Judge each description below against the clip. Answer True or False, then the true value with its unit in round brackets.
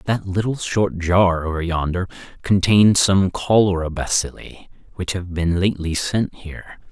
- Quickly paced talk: False (140 wpm)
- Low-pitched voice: True (90 Hz)